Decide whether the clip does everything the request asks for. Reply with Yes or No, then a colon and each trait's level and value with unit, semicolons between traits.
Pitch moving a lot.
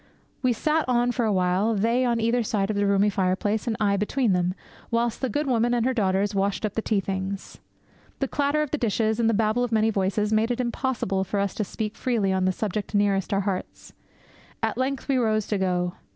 No: average, 3.4 semitones